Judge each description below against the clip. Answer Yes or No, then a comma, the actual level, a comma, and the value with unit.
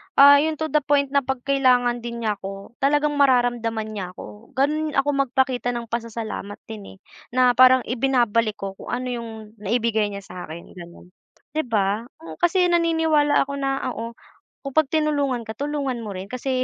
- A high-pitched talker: Yes, high, 245 Hz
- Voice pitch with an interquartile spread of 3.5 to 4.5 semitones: Yes, average, 4.2 semitones